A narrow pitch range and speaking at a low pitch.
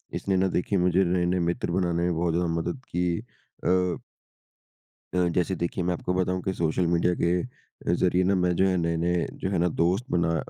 Yes: narrow, 1.2 semitones; very low, 90 Hz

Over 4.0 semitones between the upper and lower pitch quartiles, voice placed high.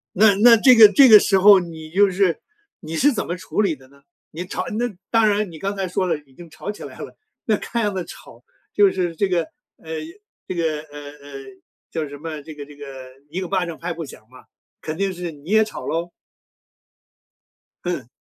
No: average, 4.4 semitones; medium, 175 Hz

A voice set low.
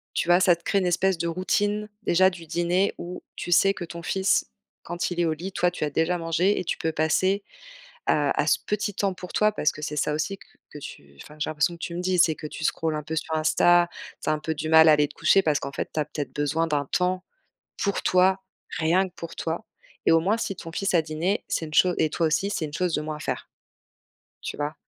No: medium, 170 Hz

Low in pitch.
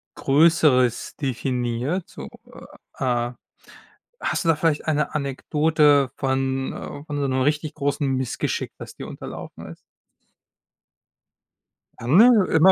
No: medium, 145 Hz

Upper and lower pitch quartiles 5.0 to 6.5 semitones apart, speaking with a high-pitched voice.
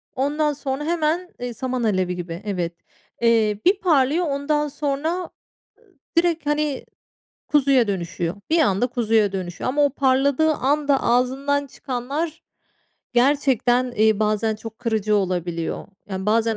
Yes: wide, 5.5 semitones; very high, 255 Hz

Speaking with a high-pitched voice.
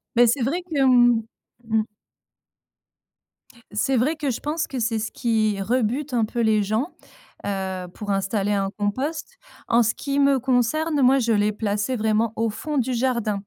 Yes: high, 235 Hz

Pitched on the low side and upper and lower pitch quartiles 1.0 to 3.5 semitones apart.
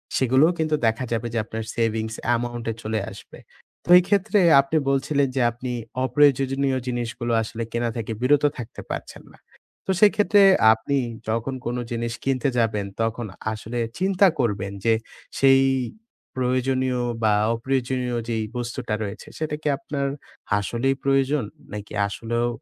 Yes: low, 125 Hz; average, 3.0 semitones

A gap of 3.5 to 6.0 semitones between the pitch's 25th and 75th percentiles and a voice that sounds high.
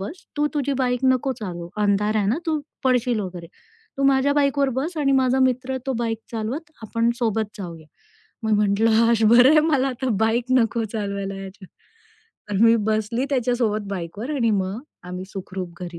Yes: average, 4.7 semitones; high, 230 Hz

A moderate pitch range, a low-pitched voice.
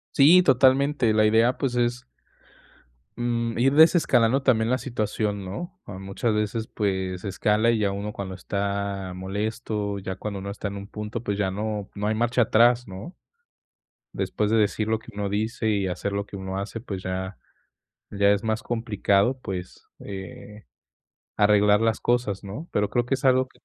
Yes: average, 3.1 semitones; low, 105 Hz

